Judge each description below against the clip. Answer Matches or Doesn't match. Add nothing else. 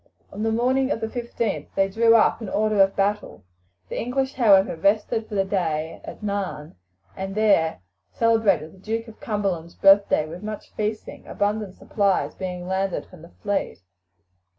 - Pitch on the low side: Doesn't match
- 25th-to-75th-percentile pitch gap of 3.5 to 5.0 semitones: Doesn't match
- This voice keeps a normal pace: Matches